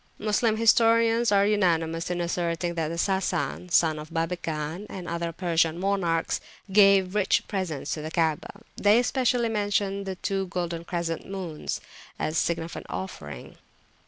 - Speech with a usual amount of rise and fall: Yes, average, 3.5 semitones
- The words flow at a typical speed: No, slow, 130 wpm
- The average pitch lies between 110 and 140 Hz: No, medium, 180 Hz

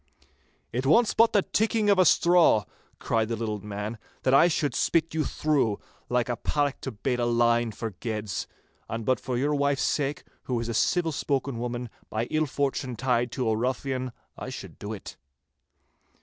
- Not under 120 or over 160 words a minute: No, average, 185 wpm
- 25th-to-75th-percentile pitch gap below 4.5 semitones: Yes, average, 4.1 semitones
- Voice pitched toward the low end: Yes, low, 125 Hz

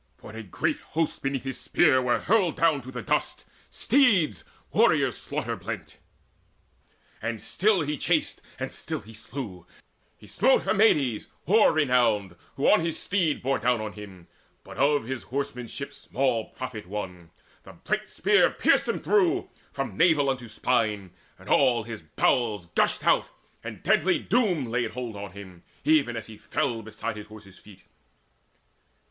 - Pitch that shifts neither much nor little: No, wide, 5.8 semitones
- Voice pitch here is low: Yes, low, 125 Hz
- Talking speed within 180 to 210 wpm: No, average, 155 wpm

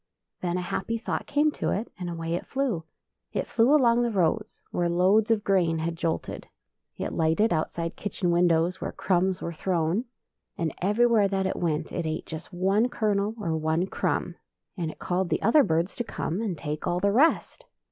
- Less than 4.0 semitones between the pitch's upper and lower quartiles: No, average, 4.3 semitones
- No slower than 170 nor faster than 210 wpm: Yes, average, 190 wpm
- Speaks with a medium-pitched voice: Yes, medium, 180 Hz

